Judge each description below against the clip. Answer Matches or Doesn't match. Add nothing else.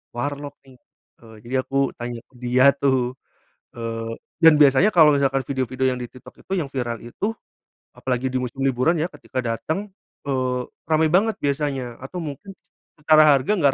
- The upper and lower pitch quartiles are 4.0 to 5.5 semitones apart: Doesn't match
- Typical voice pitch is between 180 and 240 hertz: Doesn't match